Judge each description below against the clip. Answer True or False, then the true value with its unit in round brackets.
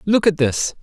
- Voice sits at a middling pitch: True (170 Hz)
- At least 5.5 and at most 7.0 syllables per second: False (4.5 syllables/s)